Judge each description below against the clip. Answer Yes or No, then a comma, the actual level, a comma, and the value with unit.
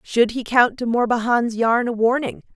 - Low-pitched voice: No, high, 235 Hz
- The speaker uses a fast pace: No, average, 190 wpm